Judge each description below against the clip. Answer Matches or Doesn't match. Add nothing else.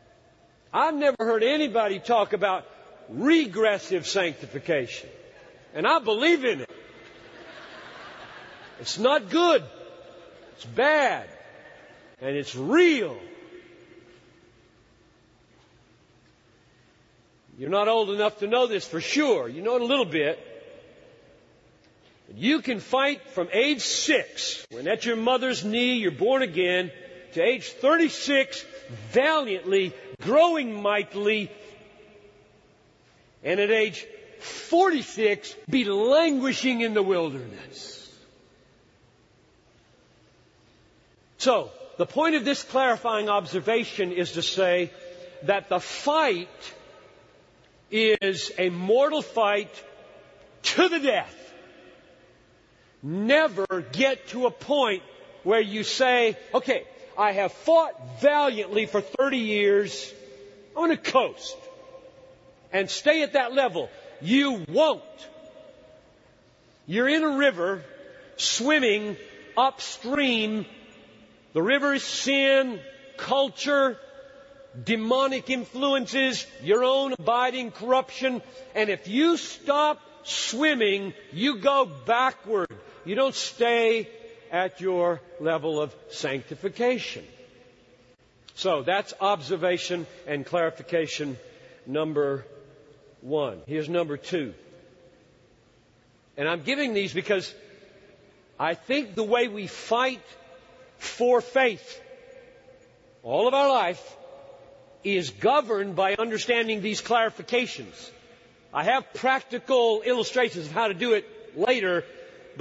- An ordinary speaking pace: Doesn't match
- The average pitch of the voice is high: Matches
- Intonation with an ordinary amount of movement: Doesn't match